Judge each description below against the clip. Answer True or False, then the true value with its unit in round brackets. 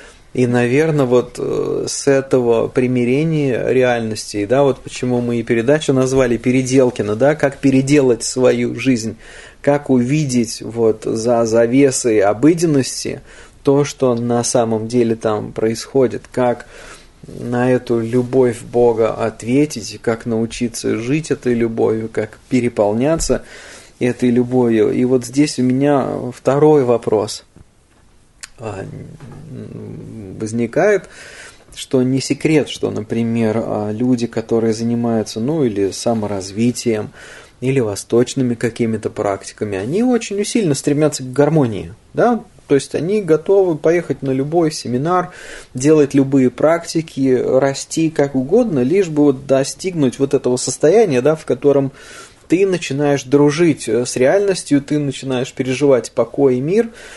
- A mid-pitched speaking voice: False (130 Hz)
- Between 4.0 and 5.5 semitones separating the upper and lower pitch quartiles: False (3.5 semitones)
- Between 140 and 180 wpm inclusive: False (120 wpm)